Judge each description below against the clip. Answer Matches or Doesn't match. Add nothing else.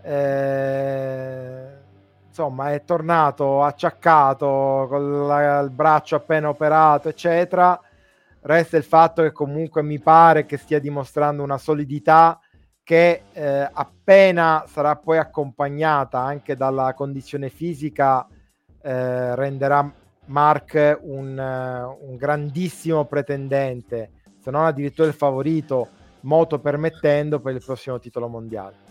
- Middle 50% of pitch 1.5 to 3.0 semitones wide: Matches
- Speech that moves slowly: Matches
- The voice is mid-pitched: Matches